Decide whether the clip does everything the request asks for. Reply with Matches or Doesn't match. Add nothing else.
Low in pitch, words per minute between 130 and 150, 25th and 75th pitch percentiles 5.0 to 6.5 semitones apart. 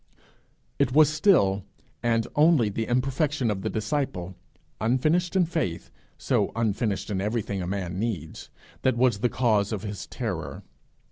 Matches